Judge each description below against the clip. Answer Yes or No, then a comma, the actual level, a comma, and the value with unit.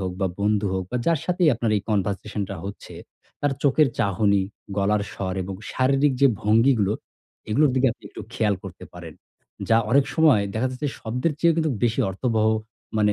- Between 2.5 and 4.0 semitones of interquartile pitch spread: No, average, 5.2 semitones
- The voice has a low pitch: Yes, low, 110 Hz